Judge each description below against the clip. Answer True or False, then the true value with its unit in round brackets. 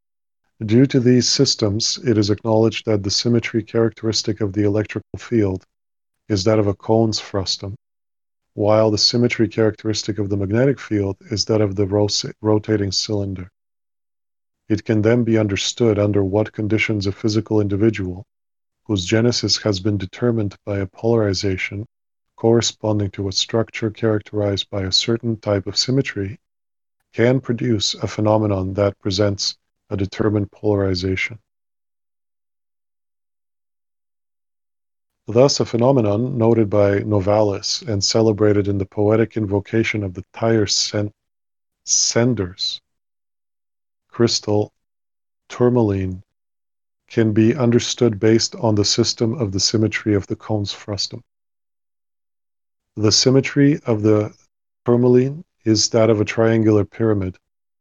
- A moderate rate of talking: False (120 wpm)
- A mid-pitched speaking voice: False (110 Hz)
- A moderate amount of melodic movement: False (2.0 semitones)